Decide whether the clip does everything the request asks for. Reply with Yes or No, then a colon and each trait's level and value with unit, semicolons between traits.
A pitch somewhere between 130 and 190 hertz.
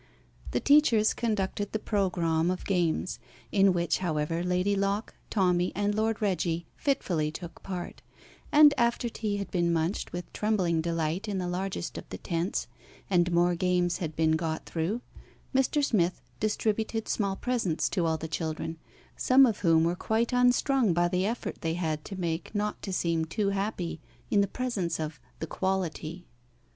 Yes: medium, 185 Hz